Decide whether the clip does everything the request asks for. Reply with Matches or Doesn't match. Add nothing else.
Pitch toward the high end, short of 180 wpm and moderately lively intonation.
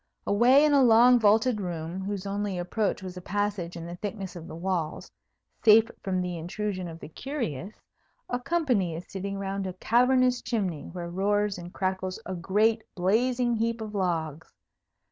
Matches